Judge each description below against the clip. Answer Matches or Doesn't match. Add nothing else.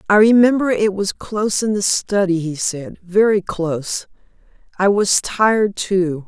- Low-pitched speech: Doesn't match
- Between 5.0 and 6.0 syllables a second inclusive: Doesn't match